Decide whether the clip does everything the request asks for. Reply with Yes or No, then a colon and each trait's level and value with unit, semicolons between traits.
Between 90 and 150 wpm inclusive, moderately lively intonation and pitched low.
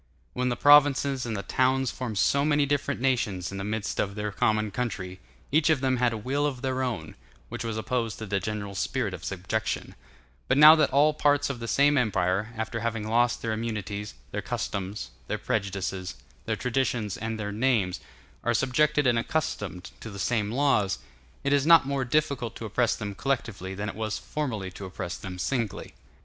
No: average, 195 wpm; average, 4.6 semitones; low, 115 Hz